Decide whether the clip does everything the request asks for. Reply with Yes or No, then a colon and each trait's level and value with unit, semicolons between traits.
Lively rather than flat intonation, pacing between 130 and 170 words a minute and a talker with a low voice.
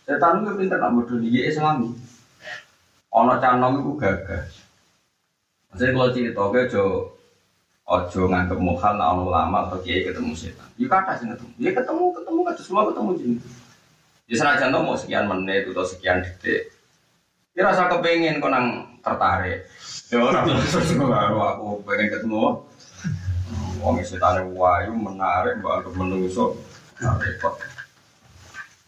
Yes: wide, 8.7 semitones; average, 135 wpm; low, 120 Hz